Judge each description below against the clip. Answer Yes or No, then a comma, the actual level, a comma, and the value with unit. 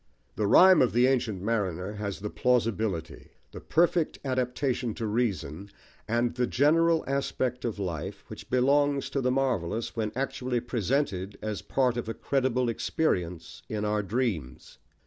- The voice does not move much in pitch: No, average, 4.3 semitones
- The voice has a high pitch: No, low, 120 Hz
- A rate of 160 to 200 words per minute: No, average, 145 wpm